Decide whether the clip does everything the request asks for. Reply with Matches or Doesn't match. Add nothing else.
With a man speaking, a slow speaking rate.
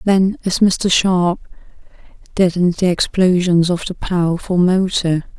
Doesn't match